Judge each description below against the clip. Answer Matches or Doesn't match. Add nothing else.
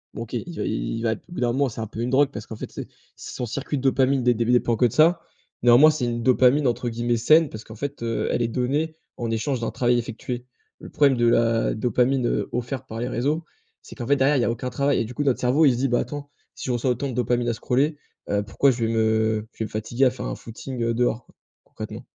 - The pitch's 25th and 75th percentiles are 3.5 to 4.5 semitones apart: Doesn't match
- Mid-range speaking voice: Doesn't match